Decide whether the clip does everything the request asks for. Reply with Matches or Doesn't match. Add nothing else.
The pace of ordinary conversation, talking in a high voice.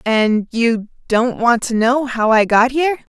Matches